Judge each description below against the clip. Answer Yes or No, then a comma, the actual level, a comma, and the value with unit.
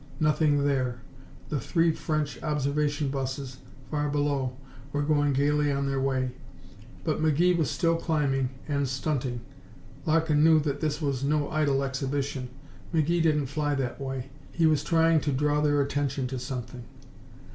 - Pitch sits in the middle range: Yes, medium, 145 Hz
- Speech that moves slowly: No, average, 150 wpm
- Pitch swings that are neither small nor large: No, narrow, 2.2 semitones